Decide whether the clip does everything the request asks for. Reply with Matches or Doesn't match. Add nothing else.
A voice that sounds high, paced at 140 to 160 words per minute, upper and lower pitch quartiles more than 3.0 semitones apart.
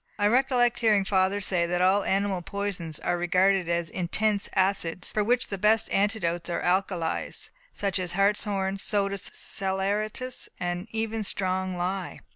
Doesn't match